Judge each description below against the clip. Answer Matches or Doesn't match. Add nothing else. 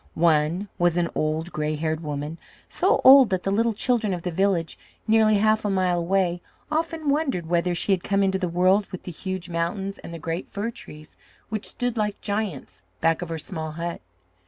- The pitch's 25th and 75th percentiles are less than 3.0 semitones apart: Doesn't match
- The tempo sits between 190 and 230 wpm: Matches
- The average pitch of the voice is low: Doesn't match